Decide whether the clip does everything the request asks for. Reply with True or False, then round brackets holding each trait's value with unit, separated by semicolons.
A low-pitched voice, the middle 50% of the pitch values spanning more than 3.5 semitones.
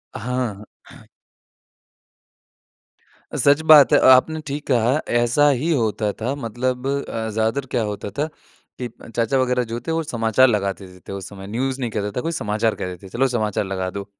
True (120 Hz; 3.9 semitones)